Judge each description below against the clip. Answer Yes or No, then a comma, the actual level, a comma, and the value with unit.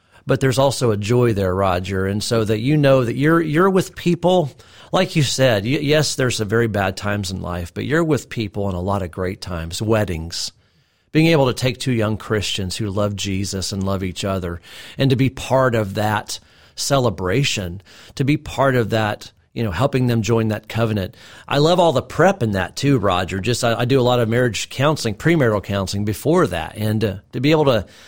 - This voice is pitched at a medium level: No, low, 115 Hz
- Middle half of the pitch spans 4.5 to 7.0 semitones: Yes, average, 5.3 semitones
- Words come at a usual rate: No, fast, 215 wpm